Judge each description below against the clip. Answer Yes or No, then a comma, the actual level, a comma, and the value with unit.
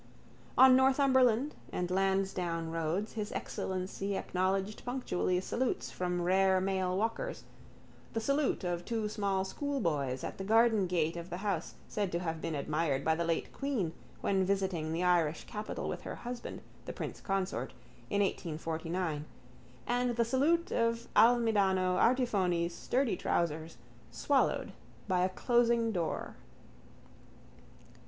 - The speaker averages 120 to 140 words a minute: Yes, slow, 135 wpm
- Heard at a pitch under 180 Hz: No, high, 190 Hz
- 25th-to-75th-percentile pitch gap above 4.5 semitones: Yes, average, 5.0 semitones